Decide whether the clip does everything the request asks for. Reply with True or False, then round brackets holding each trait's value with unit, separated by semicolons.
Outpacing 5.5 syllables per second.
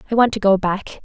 True (6.2 syllables/s)